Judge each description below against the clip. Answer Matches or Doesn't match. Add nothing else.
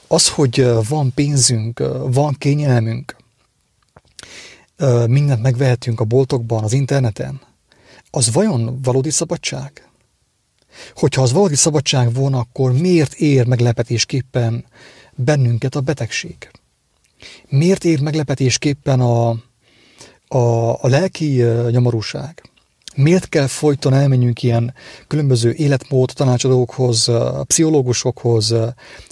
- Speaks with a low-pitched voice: Matches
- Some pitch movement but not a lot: Matches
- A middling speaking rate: Doesn't match